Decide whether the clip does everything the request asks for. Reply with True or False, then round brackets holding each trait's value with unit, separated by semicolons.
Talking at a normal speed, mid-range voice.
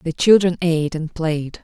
True (185 wpm; 165 Hz)